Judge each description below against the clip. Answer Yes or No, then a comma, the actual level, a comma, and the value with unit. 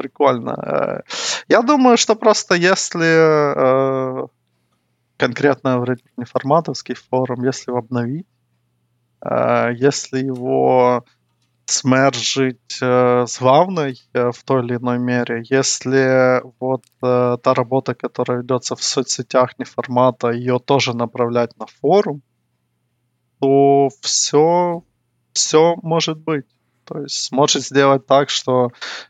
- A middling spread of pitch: No, narrow, 2.2 semitones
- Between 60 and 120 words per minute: Yes, average, 110 wpm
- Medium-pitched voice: No, low, 130 Hz